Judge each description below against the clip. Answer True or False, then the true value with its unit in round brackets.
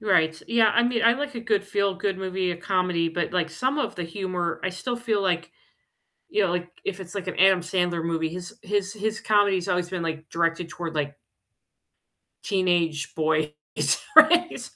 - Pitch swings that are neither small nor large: True (3.5 semitones)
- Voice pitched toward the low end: False (185 Hz)